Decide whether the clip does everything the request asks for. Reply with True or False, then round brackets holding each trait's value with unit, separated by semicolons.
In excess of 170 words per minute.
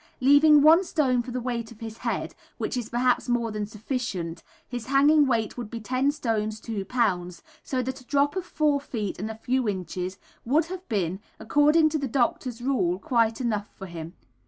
True (195 wpm)